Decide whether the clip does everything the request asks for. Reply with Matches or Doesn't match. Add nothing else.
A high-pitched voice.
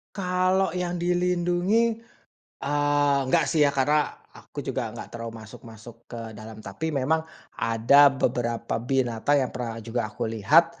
Doesn't match